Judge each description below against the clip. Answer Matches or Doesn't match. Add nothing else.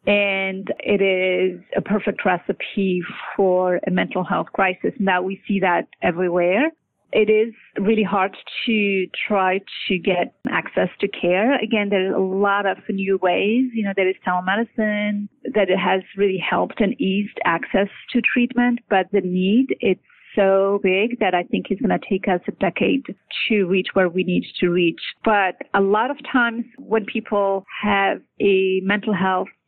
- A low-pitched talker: Doesn't match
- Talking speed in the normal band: Matches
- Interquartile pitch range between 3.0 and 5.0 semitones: Doesn't match